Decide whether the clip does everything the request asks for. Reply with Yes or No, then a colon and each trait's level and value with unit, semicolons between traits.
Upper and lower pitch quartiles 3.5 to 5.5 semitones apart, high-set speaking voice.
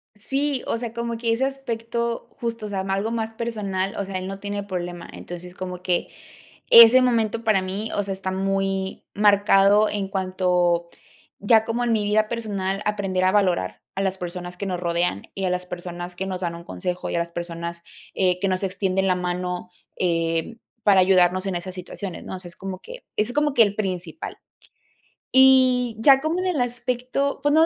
Yes: average, 4.0 semitones; high, 195 Hz